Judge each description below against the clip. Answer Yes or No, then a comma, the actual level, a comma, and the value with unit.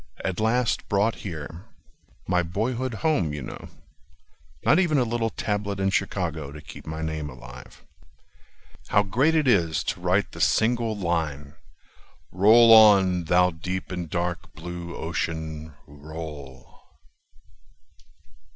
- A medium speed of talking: No, slow, 125 wpm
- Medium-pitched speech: No, very low, 90 Hz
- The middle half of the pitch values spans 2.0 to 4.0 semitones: No, wide, 5.6 semitones